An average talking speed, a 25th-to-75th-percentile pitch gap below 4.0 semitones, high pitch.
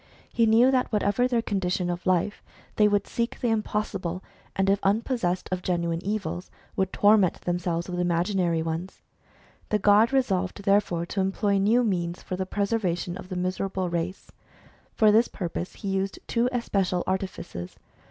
Yes: average, 160 wpm; average, 3.0 semitones; high, 195 Hz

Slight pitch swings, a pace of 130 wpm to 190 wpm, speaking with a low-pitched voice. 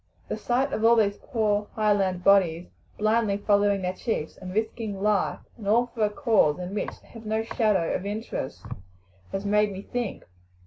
No: narrow, 2.2 semitones; average, 180 wpm; high, 210 Hz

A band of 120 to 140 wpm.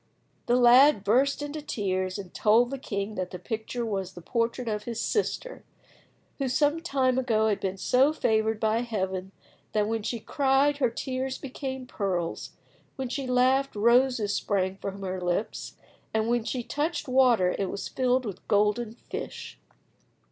No: average, 160 wpm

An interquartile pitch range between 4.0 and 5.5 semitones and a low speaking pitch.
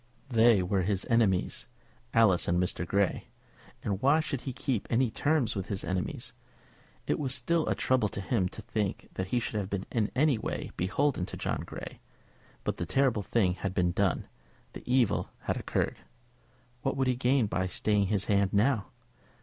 Yes: average, 5.0 semitones; low, 105 Hz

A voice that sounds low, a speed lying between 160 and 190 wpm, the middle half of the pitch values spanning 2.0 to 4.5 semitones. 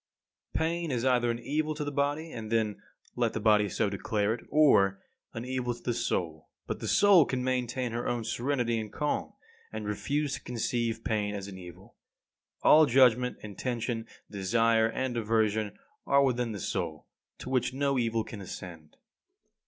Yes: low, 115 Hz; average, 175 wpm; average, 3.4 semitones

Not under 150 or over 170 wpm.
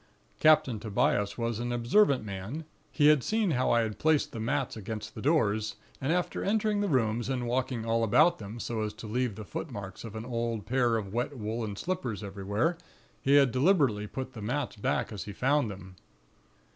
No: average, 195 wpm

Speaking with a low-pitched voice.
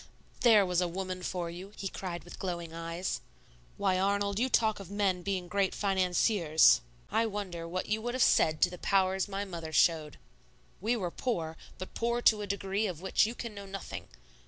No: high, 190 Hz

